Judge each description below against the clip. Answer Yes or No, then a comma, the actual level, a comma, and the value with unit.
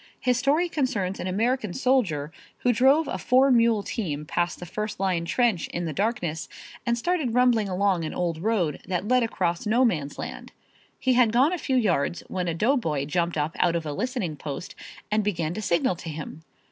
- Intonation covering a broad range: Yes, wide, 6.6 semitones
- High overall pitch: Yes, high, 200 Hz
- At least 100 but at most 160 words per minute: No, average, 195 wpm